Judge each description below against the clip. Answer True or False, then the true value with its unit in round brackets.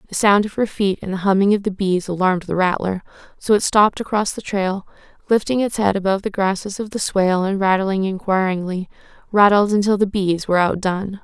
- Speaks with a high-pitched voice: True (195 Hz)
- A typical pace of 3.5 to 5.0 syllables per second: False (5.9 syllables/s)